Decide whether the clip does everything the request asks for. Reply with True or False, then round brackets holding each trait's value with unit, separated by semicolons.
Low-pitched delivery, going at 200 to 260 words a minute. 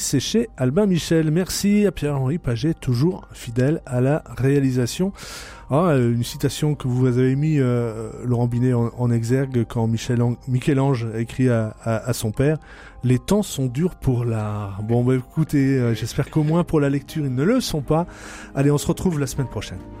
False (130 Hz; 185 wpm)